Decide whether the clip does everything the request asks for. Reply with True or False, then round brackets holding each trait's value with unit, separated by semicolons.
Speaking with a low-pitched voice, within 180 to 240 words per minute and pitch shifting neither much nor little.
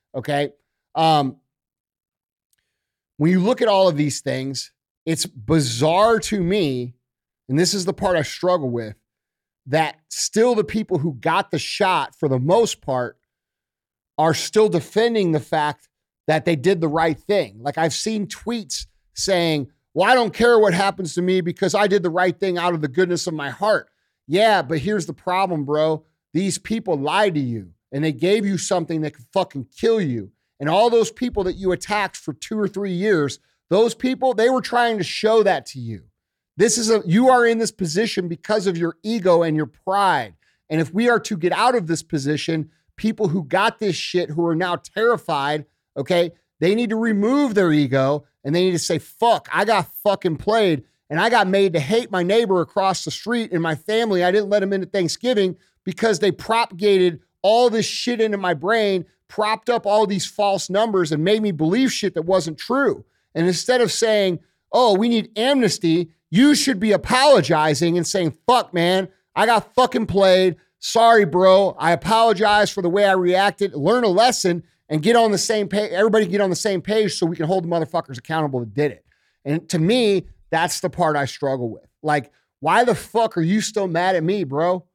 False (185 Hz; 200 wpm; 5.0 semitones)